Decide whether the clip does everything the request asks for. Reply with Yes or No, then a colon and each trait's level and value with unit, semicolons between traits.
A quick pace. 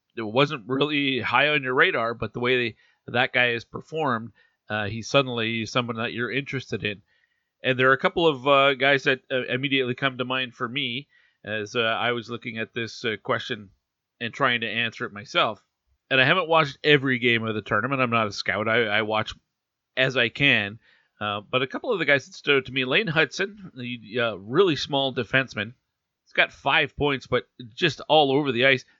Yes: fast, 210 wpm